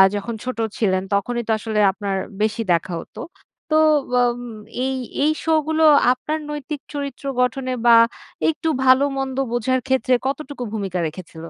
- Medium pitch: No, very high, 255 Hz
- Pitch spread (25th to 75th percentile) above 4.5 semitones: Yes, average, 4.9 semitones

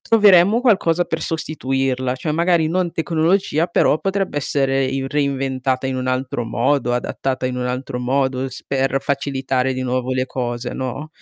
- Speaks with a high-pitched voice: No, low, 135 Hz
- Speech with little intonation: No, average, 3.8 semitones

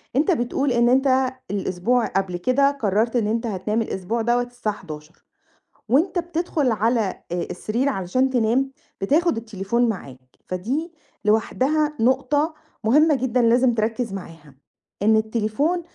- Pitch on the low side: No, high, 235 Hz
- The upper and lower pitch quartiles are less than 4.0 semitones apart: No, average, 4.3 semitones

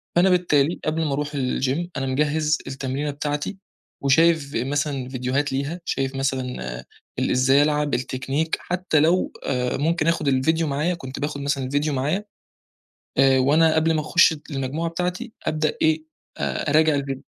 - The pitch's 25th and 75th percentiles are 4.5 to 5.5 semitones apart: No, average, 2.9 semitones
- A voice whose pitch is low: No, medium, 145 Hz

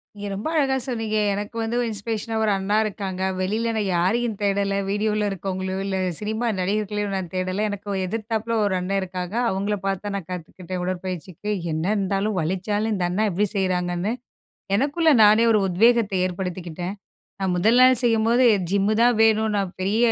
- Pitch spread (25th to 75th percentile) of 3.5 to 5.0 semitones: No, average, 2.8 semitones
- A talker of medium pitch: No, high, 200 Hz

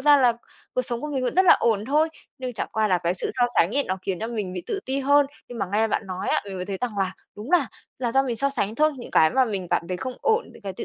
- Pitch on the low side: No, high, 235 Hz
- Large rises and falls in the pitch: Yes, wide, 5.8 semitones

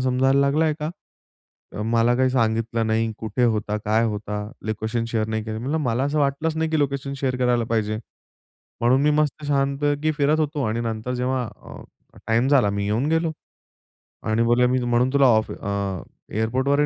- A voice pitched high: No, low, 125 Hz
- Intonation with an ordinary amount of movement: Yes, average, 4.0 semitones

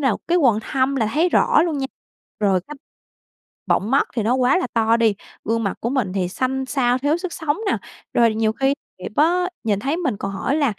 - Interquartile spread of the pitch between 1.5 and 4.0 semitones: No, average, 4.7 semitones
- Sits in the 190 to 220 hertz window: No, very high, 255 Hz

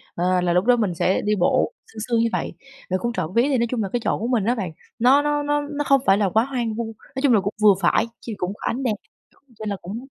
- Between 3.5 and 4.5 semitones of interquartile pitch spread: Yes, average, 4.2 semitones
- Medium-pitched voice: No, high, 225 Hz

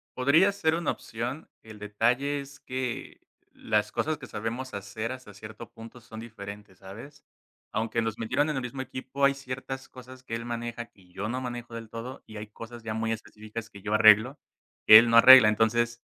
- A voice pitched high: No, low, 115 Hz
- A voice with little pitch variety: No, average, 3.0 semitones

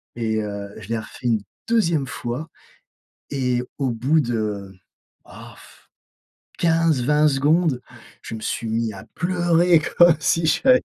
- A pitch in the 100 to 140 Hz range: Yes, low, 135 Hz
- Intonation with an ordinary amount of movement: No, wide, 6.5 semitones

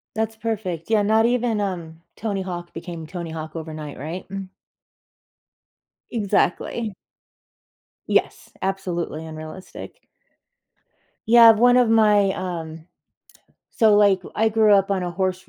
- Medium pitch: No, high, 195 Hz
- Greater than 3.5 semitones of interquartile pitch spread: Yes, average, 4.4 semitones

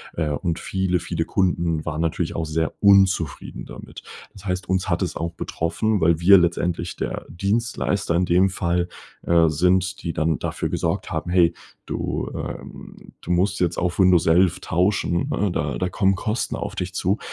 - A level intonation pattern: Yes, narrow, 2.3 semitones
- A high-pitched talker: No, very low, 90 Hz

